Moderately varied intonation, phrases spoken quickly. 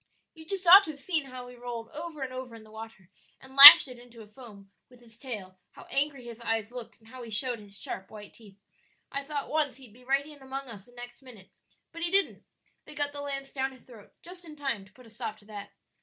Yes: average, 4.0 semitones; fast, 255 wpm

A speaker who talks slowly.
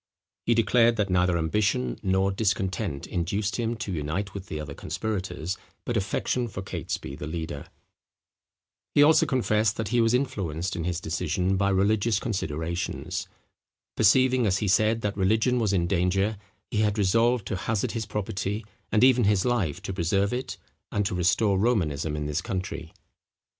No: average, 165 wpm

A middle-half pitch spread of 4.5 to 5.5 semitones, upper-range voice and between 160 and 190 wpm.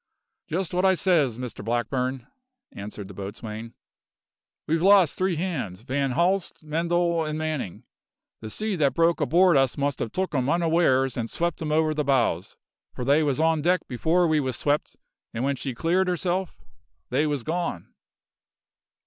No: average, 5.1 semitones; medium, 150 Hz; average, 165 wpm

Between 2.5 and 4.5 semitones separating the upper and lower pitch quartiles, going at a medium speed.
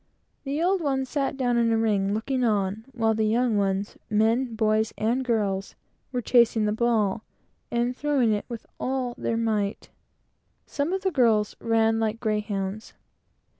Yes: average, 2.8 semitones; average, 160 wpm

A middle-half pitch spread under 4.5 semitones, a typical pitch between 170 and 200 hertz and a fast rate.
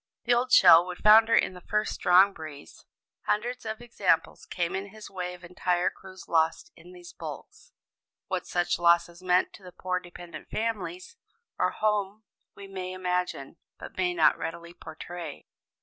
No: average, 3.5 semitones; medium, 185 Hz; average, 165 wpm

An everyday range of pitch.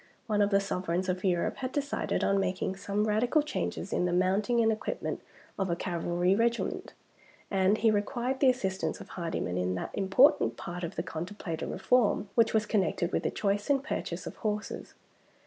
Yes: average, 3.9 semitones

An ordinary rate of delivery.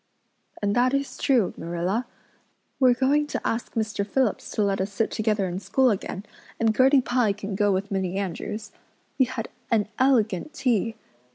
Yes: average, 170 wpm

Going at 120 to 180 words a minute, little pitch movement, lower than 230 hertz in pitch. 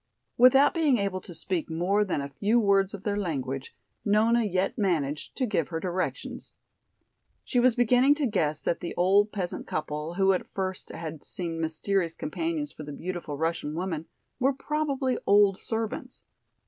No: average, 165 wpm; wide, 5.6 semitones; high, 190 Hz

